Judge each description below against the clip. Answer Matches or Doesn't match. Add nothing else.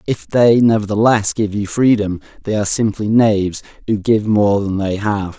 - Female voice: Doesn't match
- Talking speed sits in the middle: Matches